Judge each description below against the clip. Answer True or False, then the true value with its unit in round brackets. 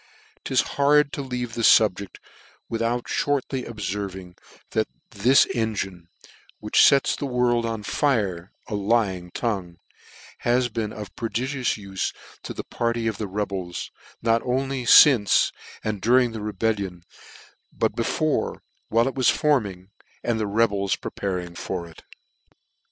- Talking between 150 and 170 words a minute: False (140 wpm)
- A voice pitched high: False (110 Hz)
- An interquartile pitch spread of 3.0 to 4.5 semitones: True (3.9 semitones)